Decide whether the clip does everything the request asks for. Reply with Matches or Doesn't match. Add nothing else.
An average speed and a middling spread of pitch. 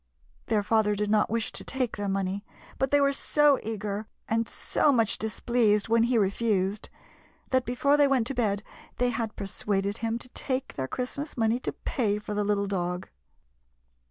Matches